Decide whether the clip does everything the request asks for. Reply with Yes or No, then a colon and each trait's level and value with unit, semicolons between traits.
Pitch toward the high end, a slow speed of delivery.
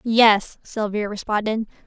Yes: high, 215 Hz; slow, 95 wpm